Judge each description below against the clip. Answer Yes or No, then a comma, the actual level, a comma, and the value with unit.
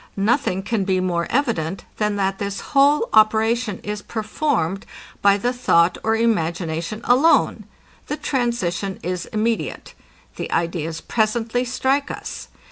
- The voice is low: No, high, 215 Hz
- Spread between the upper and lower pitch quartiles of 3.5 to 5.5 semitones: Yes, average, 4.5 semitones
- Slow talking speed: Yes, slow, 125 wpm